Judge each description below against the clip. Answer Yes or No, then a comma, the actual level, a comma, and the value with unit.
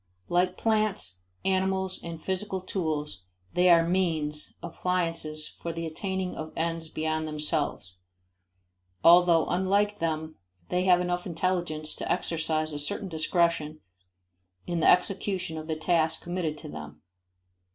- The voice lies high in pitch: No, medium, 165 Hz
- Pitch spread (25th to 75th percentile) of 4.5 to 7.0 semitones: No, average, 2.7 semitones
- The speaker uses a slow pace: Yes, slow, 130 wpm